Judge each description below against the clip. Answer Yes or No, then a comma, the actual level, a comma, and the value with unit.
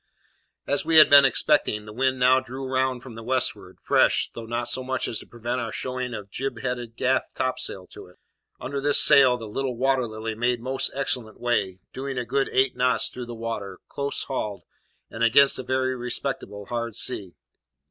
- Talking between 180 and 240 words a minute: Yes, average, 200 wpm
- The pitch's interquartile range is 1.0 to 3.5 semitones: Yes, narrow, 2.5 semitones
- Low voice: Yes, low, 125 Hz